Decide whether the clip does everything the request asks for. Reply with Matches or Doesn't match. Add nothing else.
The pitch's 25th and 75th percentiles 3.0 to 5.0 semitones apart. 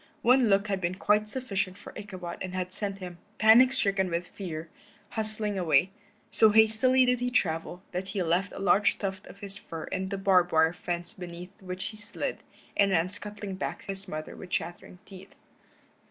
Doesn't match